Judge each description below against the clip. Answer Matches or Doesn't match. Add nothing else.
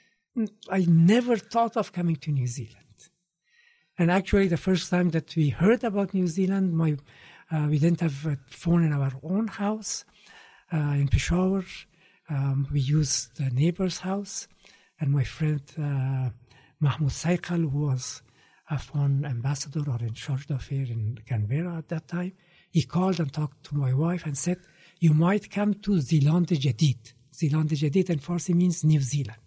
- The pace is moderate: Doesn't match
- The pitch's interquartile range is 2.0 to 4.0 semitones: Doesn't match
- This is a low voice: Doesn't match